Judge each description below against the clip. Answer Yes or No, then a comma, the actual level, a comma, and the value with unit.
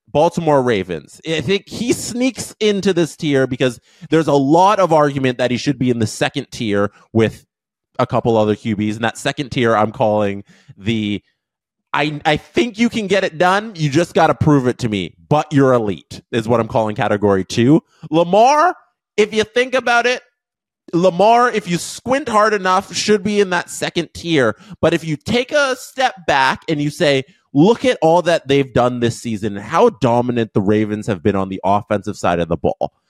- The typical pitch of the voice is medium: Yes, medium, 145 Hz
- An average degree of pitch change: No, wide, 8.8 semitones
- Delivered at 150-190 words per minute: No, average, 200 wpm